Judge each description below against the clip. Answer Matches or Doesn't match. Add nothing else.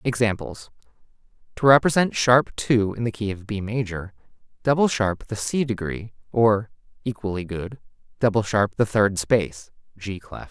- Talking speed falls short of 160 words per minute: Matches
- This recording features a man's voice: Matches